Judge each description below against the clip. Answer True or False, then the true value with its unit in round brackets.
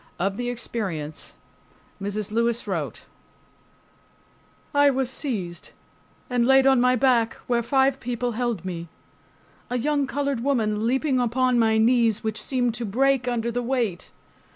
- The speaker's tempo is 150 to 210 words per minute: False (140 wpm)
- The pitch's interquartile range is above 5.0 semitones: False (2.9 semitones)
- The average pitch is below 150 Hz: False (240 Hz)